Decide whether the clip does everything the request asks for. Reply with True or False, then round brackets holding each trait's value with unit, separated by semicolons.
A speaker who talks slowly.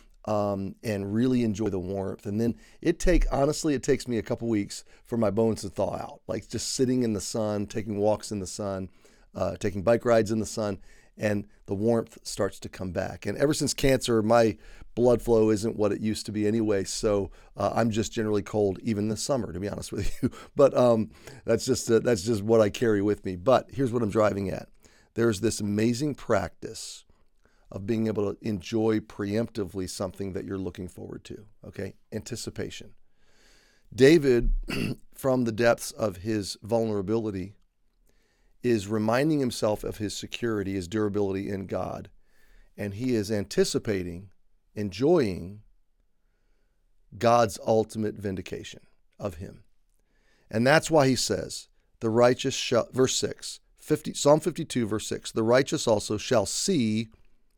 False (165 wpm)